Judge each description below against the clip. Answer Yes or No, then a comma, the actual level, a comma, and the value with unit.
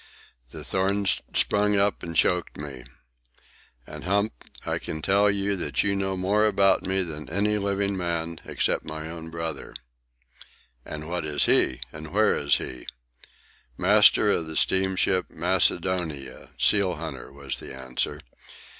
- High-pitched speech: No, very low, 90 Hz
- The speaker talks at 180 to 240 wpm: No, average, 145 wpm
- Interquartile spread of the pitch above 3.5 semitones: Yes, average, 4.0 semitones